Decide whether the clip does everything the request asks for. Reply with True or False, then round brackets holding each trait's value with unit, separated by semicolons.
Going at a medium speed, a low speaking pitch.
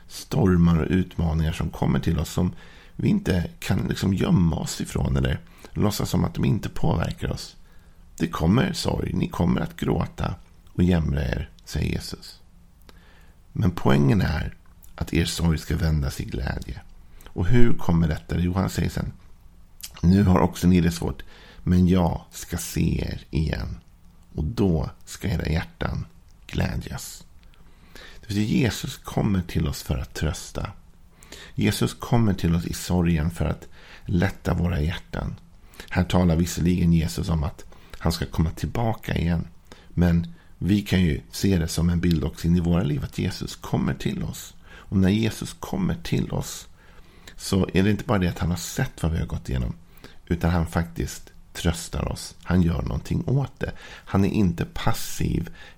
True (165 wpm; 85 Hz)